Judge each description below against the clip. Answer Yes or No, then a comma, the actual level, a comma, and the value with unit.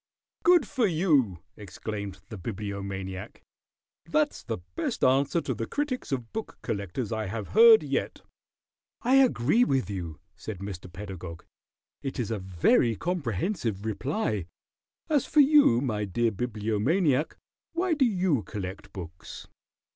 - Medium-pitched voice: No, low, 115 Hz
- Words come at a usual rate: No, slow, 130 wpm